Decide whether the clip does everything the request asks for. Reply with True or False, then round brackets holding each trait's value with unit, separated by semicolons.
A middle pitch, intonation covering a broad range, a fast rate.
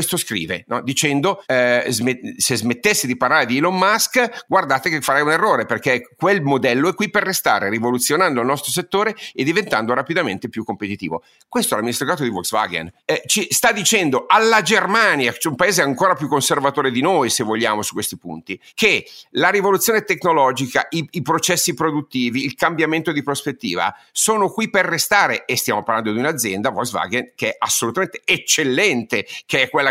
True (150 Hz; 7.6 semitones; 180 wpm)